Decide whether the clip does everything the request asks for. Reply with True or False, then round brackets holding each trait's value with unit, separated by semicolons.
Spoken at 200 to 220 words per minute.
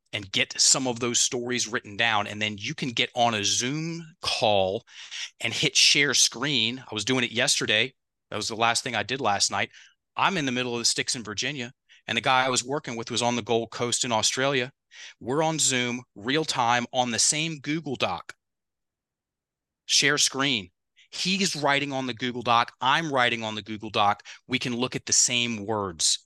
True (205 wpm)